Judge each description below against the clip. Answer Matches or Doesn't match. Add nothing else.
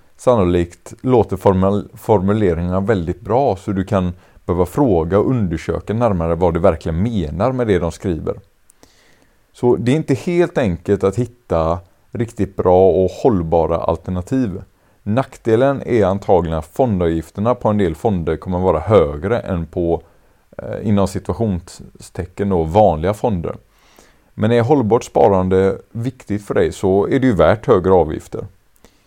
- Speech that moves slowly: Doesn't match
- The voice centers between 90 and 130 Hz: Matches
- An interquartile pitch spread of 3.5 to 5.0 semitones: Matches